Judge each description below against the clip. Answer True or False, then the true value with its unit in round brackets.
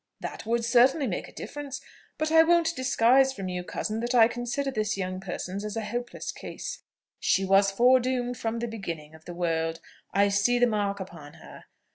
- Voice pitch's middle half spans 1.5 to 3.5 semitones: False (4.5 semitones)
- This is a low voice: False (225 Hz)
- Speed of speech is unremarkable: True (190 wpm)